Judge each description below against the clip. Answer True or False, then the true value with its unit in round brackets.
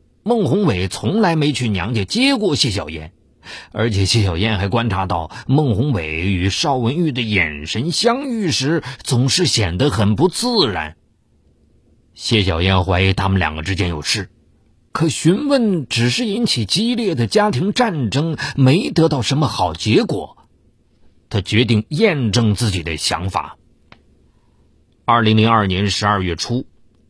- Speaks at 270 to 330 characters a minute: False (215 characters per minute)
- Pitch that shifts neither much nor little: False (8.0 semitones)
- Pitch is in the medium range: False (115 Hz)